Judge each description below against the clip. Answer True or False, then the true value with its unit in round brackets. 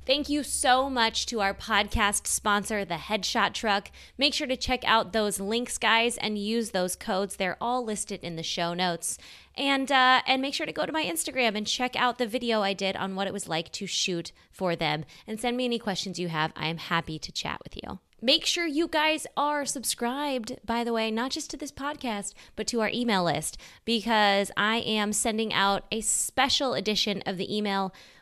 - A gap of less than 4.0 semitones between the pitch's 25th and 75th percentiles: False (4.4 semitones)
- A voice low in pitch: False (220 Hz)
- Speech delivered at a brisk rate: True (215 wpm)